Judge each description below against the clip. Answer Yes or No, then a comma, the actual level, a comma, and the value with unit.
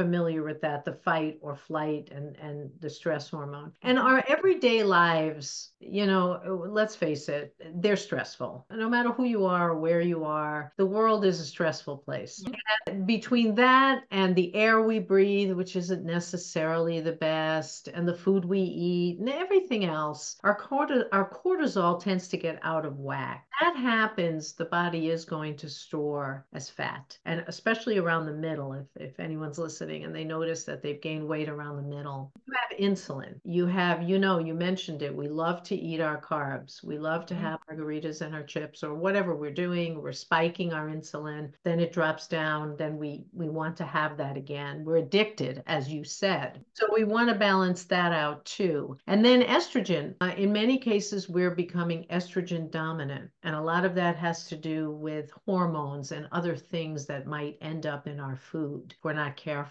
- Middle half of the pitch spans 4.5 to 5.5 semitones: No, average, 3.9 semitones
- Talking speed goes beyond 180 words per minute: Yes, average, 190 wpm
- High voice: No, medium, 165 Hz